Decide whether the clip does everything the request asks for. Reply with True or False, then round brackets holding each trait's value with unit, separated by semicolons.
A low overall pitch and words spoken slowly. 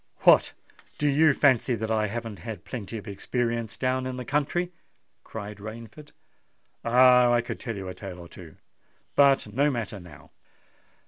False (115 Hz; 155 wpm)